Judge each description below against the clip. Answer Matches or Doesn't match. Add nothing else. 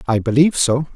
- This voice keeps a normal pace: Matches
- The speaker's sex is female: Doesn't match